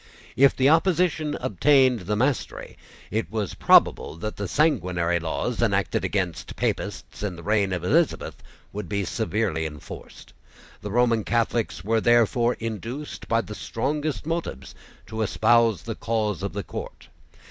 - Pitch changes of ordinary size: Yes, average, 4.6 semitones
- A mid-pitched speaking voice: No, low, 110 Hz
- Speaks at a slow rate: No, average, 145 wpm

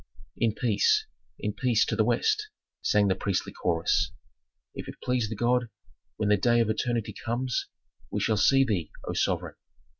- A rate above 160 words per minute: Yes, average, 170 wpm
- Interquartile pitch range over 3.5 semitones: No, average, 3.1 semitones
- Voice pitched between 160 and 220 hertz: No, low, 115 Hz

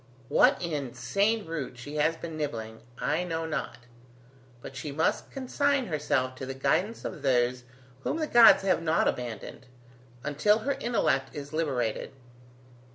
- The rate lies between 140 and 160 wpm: Yes, average, 145 wpm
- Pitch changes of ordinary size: No, wide, 6.1 semitones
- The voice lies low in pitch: No, medium, 150 Hz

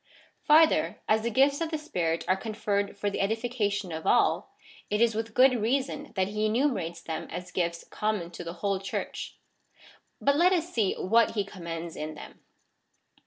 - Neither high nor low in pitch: No, high, 210 Hz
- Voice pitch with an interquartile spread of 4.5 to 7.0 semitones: Yes, wide, 5.4 semitones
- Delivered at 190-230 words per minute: No, average, 175 wpm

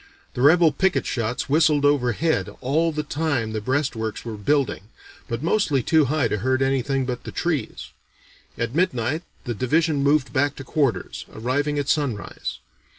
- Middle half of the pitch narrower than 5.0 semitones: Yes, average, 4.0 semitones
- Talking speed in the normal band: Yes, average, 155 wpm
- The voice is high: No, medium, 140 Hz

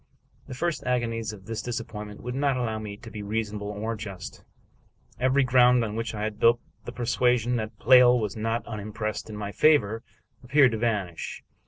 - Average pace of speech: Yes, average, 180 wpm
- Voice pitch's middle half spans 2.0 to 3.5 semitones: Yes, average, 2.7 semitones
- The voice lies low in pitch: Yes, low, 115 Hz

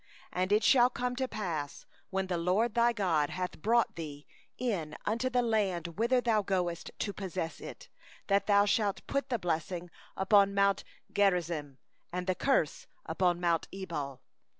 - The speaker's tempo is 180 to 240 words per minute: No, average, 155 wpm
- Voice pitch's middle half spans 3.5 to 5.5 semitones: Yes, average, 4.5 semitones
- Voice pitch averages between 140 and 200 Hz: Yes, high, 190 Hz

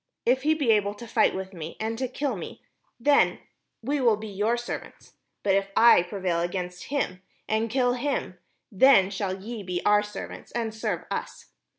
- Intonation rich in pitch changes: No, average, 4.2 semitones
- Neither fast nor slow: Yes, average, 185 wpm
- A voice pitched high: Yes, high, 215 Hz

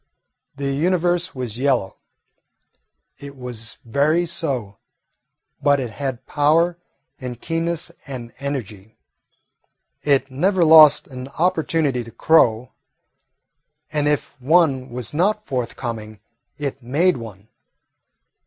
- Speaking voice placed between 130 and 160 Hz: Yes, medium, 140 Hz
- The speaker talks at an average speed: No, slow, 105 wpm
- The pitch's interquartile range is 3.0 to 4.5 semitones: No, average, 4.9 semitones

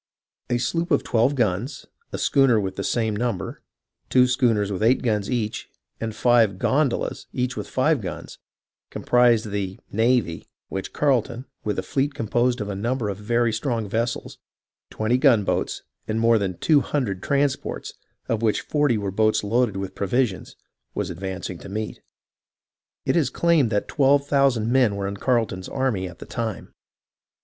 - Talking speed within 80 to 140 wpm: No, average, 165 wpm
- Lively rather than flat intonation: No, average, 3.9 semitones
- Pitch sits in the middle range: No, low, 115 Hz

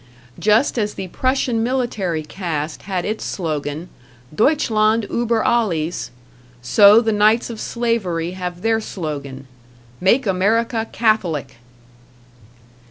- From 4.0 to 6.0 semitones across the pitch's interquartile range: Yes, average, 5.3 semitones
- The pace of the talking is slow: Yes, slow, 105 wpm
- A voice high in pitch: Yes, high, 205 Hz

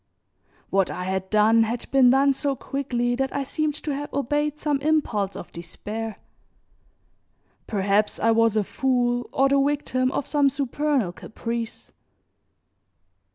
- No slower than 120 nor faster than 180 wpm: Yes, average, 140 wpm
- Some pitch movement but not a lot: Yes, average, 4.2 semitones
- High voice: Yes, very high, 250 Hz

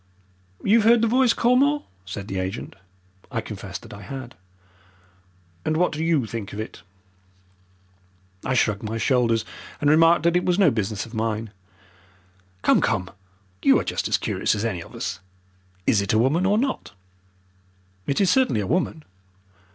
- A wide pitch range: Yes, wide, 8.9 semitones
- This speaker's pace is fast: No, average, 165 wpm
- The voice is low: Yes, low, 130 Hz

